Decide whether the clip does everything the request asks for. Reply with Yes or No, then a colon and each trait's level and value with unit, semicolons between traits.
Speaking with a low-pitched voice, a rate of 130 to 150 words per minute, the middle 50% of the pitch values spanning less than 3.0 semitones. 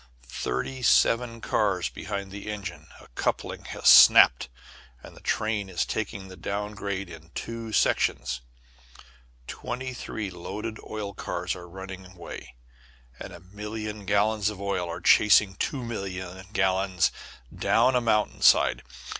Yes: low, 100 Hz; average, 140 wpm; narrow, 2.5 semitones